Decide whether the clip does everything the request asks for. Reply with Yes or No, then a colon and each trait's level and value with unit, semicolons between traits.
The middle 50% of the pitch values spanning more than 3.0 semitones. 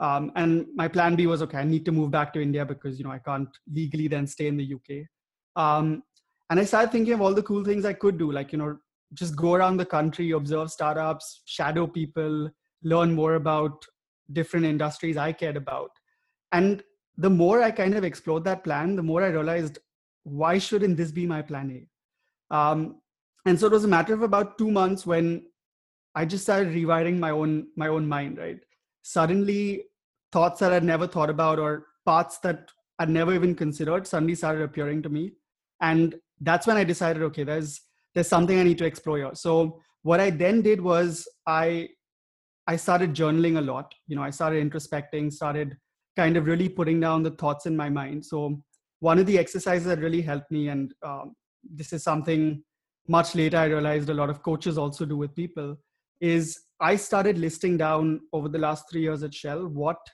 No: narrow, 2.4 semitones